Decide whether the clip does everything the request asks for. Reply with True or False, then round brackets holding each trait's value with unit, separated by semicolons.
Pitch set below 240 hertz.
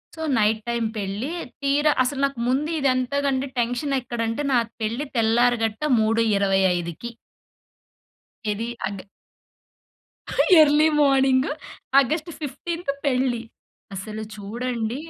False (245 Hz)